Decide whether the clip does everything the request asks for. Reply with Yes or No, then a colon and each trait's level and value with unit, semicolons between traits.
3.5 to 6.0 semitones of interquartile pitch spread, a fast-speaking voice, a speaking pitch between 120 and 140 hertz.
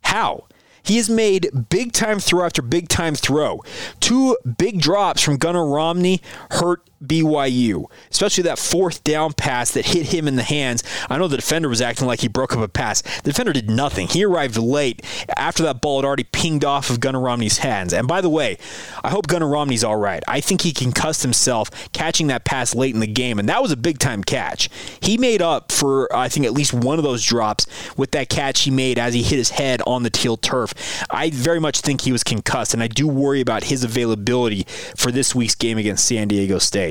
Yes: average, 4.9 semitones; fast, 220 wpm; low, 135 Hz